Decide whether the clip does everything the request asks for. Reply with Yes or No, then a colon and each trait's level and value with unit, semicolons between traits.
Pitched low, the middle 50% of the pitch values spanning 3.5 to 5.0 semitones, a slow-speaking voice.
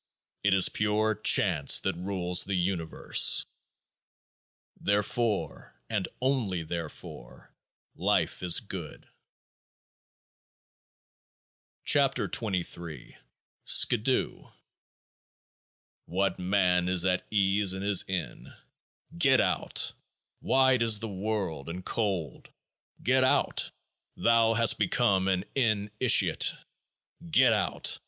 Yes: low, 100 Hz; average, 3.9 semitones; slow, 100 wpm